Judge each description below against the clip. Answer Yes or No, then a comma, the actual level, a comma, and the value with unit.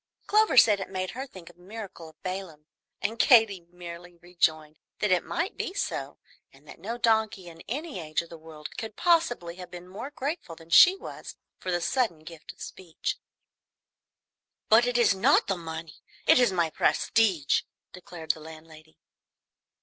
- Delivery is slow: No, average, 175 wpm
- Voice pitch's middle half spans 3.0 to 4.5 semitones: No, wide, 5.5 semitones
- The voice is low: No, medium, 185 Hz